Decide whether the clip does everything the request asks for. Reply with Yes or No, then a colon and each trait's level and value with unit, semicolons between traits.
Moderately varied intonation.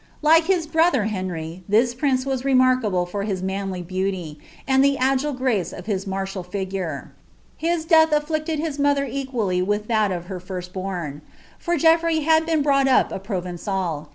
No: wide, 7.4 semitones